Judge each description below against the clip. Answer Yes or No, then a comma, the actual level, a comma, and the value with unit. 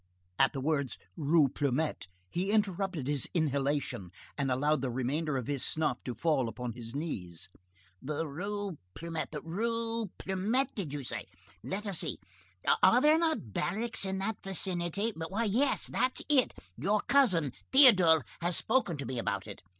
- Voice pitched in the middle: Yes, medium, 165 Hz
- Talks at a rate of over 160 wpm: No, average, 150 wpm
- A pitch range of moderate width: No, wide, 6.9 semitones